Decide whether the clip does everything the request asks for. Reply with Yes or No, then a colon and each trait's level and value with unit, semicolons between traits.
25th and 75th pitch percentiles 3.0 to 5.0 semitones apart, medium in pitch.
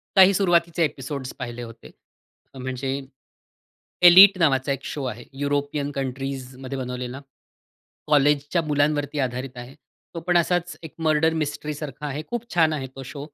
Yes: average, 3.4 semitones; medium, 145 Hz